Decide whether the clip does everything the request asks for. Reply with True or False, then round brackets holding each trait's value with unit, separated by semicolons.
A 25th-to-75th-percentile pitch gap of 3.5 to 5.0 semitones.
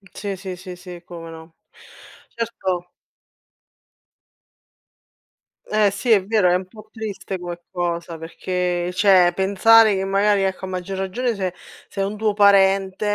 False (2.4 semitones)